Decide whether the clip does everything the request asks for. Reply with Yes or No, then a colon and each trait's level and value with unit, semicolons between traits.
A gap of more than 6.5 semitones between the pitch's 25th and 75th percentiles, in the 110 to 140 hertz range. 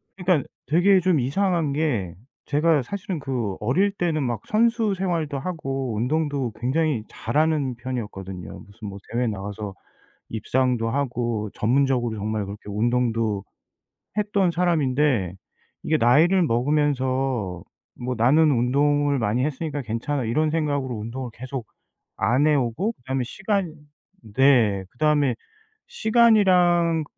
No: wide, 5.4 semitones; low, 135 Hz